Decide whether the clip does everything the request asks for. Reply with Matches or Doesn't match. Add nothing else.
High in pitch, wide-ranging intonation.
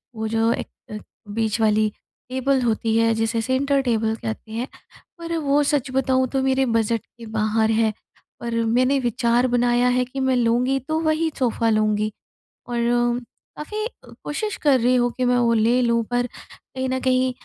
Doesn't match